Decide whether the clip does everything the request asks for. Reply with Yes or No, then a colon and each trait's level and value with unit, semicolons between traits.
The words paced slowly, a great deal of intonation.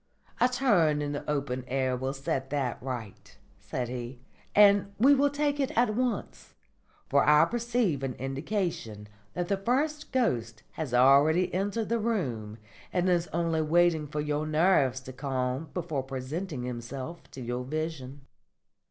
No: average, 150 wpm; wide, 7.1 semitones